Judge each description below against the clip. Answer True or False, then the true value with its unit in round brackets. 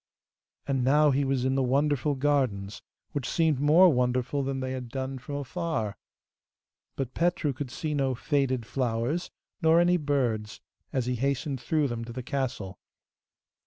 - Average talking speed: True (160 wpm)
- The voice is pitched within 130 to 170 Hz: True (135 Hz)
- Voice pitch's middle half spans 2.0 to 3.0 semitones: True (2.7 semitones)